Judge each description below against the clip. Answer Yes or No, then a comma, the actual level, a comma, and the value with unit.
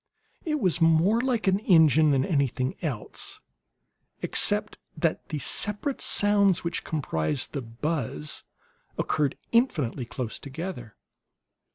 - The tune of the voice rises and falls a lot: Yes, wide, 6.9 semitones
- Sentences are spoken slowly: Yes, slow, 110 wpm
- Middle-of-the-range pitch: Yes, medium, 160 Hz